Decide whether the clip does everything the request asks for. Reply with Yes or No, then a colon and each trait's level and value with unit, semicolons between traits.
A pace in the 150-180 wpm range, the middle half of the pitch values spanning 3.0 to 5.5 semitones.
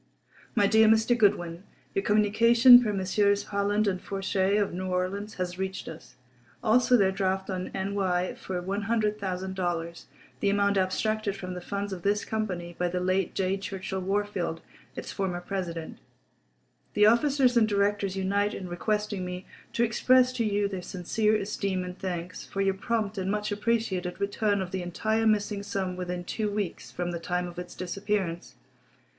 No: average, 165 wpm; narrow, 2.4 semitones